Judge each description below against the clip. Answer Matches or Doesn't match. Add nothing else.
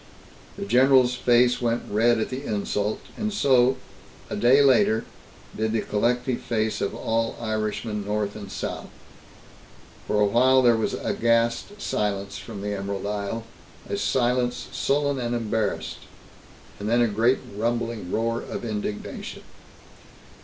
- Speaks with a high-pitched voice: Doesn't match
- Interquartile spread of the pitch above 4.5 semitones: Doesn't match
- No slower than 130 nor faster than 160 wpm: Matches